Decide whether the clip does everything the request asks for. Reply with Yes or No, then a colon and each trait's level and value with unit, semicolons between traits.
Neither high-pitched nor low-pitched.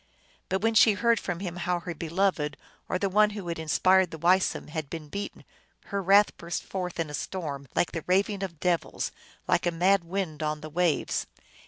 Yes: medium, 180 Hz